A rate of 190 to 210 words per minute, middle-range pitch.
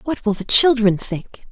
No: average, 200 wpm; high, 225 Hz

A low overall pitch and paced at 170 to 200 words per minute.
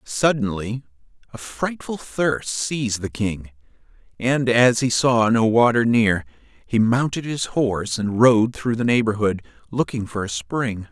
No: low, 115 Hz; average, 150 wpm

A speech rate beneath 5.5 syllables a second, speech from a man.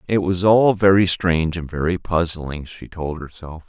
Yes: 4.6 syllables/s; male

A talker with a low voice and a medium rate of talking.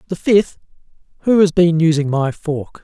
No: medium, 165 Hz; average, 170 wpm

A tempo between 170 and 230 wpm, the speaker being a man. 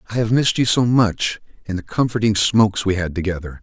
Yes: average, 200 wpm; male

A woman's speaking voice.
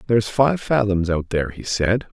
No: male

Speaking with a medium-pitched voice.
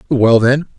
No: low, 125 Hz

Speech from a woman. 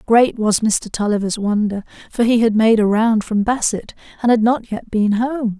Yes: female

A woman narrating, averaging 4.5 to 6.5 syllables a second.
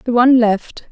Yes: female; 5.2 syllables/s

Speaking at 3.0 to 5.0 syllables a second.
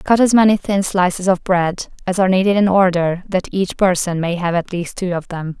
No: 5.3 syllables/s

